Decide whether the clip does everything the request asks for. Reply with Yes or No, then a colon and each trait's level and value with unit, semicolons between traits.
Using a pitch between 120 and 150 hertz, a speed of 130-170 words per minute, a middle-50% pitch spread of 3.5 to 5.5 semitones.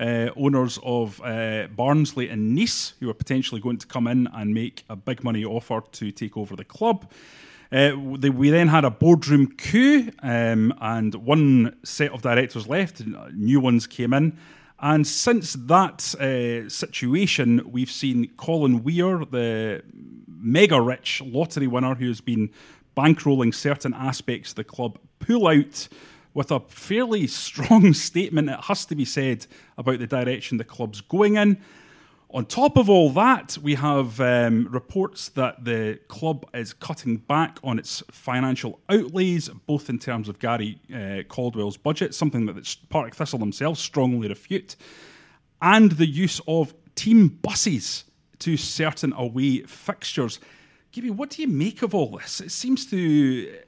Yes: low, 135 Hz; average, 160 wpm; average, 5.1 semitones